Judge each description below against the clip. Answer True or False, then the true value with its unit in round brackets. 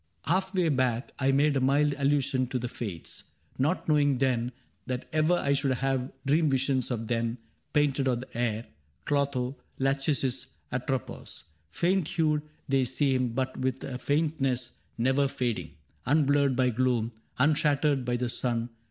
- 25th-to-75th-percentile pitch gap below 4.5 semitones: True (2.5 semitones)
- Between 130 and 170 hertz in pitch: True (135 Hz)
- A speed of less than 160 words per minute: True (150 wpm)